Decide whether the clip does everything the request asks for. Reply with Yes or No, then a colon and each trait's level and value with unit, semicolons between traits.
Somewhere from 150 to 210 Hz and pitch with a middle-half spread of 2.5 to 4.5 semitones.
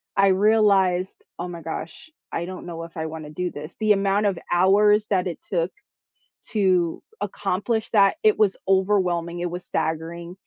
Yes: medium, 185 Hz; average, 2.9 semitones